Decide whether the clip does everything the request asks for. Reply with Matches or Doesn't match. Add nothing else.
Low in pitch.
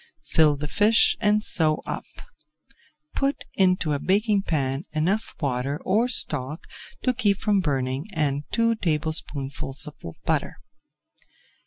Doesn't match